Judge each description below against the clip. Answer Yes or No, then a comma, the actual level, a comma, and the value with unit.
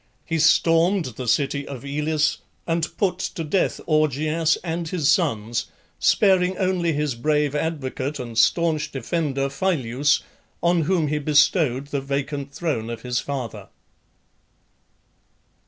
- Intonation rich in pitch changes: No, average, 3.3 semitones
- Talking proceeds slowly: Yes, slow, 125 wpm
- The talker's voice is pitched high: No, medium, 150 Hz